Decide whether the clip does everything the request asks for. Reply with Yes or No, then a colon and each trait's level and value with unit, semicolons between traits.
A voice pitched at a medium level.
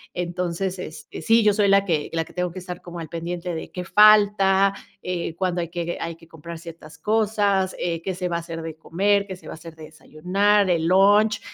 Yes: medium, 180 Hz